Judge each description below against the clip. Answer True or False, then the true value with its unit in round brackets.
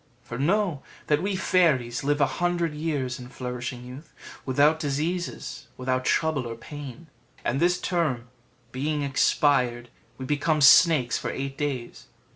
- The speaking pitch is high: False (145 Hz)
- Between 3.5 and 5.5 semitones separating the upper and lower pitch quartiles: True (3.9 semitones)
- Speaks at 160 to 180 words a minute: False (140 wpm)